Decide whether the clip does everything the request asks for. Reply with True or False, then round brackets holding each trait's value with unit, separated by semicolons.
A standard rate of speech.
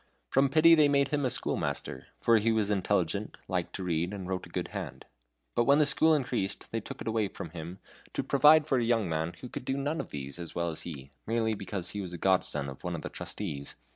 False (245 wpm)